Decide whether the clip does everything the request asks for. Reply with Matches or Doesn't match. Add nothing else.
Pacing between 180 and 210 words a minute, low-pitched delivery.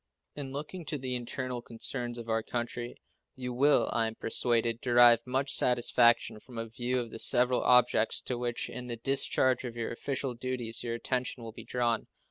Matches